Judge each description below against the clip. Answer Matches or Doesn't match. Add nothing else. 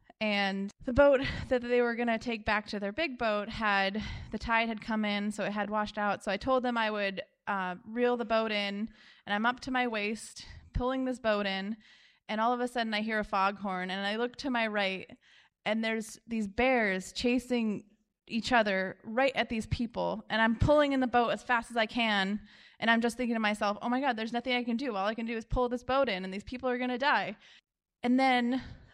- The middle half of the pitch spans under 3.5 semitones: Matches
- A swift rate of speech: Matches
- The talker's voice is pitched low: Doesn't match